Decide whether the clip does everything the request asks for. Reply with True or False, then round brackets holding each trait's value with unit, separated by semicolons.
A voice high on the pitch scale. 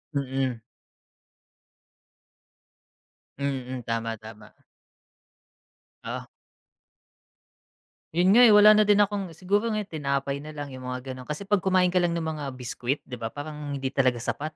False (145 Hz)